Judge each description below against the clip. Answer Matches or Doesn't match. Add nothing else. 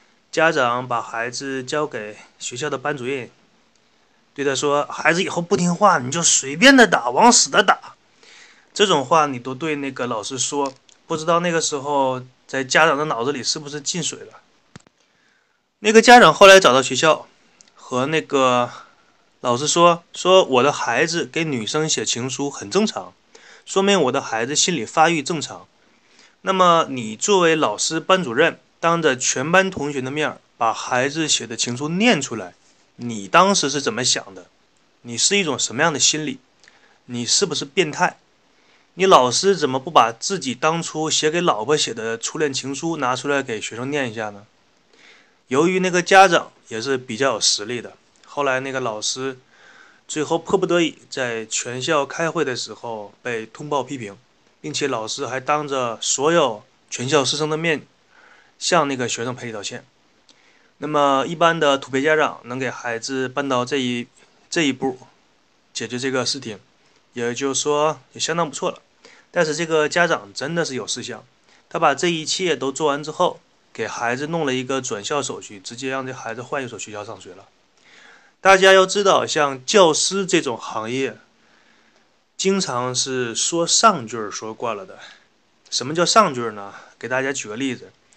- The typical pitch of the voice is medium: Matches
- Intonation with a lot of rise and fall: Doesn't match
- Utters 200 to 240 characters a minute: Doesn't match